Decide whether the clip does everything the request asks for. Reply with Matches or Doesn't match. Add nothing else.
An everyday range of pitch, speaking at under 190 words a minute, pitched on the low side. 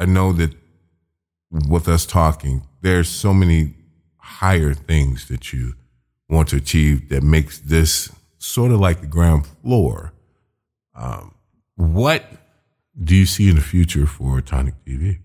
Matches